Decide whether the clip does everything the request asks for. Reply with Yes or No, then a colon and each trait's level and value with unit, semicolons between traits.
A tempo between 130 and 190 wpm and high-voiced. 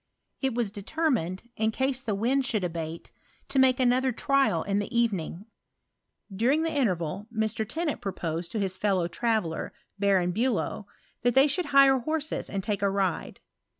Yes: average, 170 wpm; high, 220 Hz